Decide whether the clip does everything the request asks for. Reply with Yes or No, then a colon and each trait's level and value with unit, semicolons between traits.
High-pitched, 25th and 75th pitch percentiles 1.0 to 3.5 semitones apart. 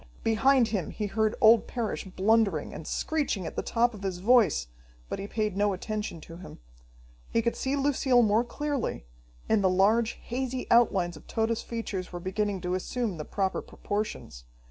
No: high, 215 Hz; average, 3.9 semitones